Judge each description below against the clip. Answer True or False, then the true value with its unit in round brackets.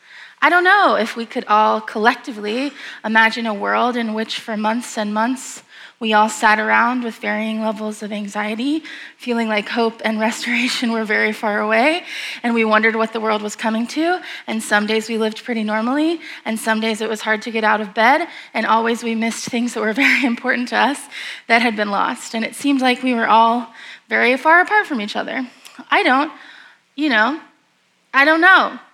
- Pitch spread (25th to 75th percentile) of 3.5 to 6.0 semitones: False (3.1 semitones)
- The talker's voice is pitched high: True (230 Hz)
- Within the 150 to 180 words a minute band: False (200 wpm)